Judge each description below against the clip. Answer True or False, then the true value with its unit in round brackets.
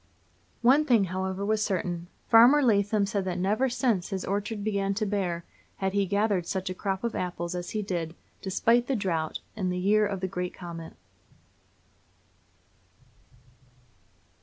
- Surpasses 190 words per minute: False (155 wpm)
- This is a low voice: False (195 Hz)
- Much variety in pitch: False (2.9 semitones)